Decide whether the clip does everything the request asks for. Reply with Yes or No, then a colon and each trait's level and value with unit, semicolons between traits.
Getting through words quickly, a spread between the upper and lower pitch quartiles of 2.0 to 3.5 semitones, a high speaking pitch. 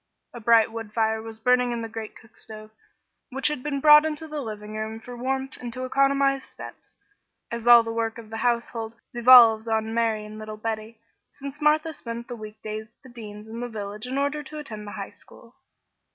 Yes: fast, 210 wpm; average, 3.1 semitones; high, 230 Hz